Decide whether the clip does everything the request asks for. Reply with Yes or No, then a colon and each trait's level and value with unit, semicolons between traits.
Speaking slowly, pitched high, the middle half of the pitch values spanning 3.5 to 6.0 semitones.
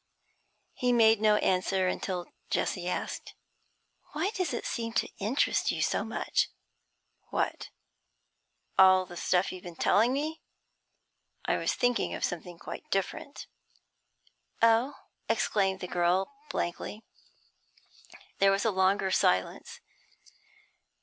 Yes: slow, 115 wpm; high, 195 Hz; average, 4.2 semitones